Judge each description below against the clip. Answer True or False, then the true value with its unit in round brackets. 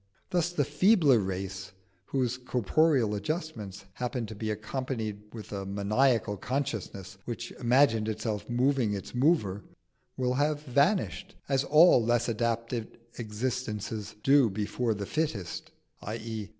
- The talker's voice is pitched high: False (115 Hz)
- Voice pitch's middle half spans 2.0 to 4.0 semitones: False (4.6 semitones)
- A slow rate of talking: True (125 wpm)